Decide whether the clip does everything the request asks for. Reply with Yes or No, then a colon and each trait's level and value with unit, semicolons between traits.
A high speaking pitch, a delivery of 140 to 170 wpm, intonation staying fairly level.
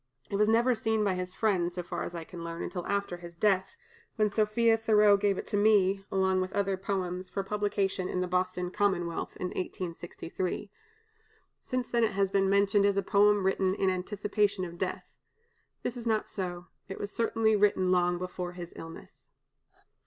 No: high, 195 Hz; average, 185 wpm; narrow, 2.3 semitones